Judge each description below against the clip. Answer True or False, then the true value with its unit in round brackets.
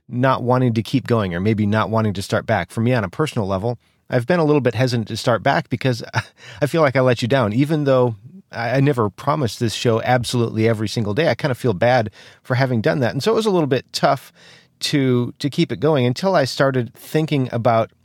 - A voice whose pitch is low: True (125 Hz)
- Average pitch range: True (3.5 semitones)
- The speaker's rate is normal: False (245 wpm)